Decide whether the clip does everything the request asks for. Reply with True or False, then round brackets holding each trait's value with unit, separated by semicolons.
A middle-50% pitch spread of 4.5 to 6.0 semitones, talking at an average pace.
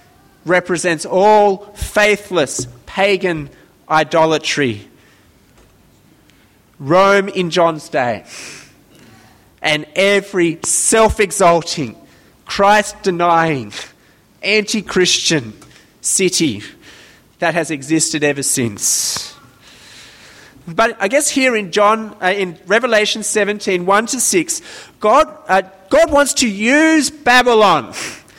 False (4.9 semitones; 80 wpm)